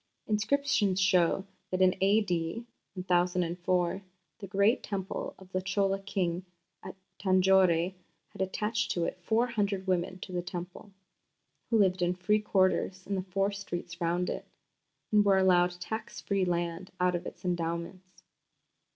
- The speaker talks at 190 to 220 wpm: No, average, 145 wpm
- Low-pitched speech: No, medium, 185 Hz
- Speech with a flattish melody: Yes, narrow, 2.0 semitones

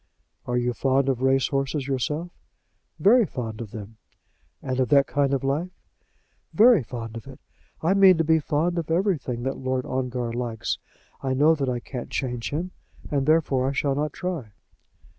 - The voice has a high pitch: No, low, 135 Hz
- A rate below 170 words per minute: No, average, 180 wpm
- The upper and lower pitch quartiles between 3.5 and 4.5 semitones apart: Yes, average, 4.2 semitones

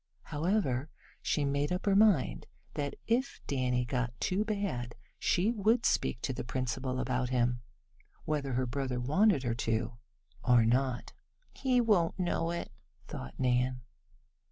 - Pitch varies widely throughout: Yes, wide, 6.7 semitones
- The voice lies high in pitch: No, low, 135 Hz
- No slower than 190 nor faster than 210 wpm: No, average, 140 wpm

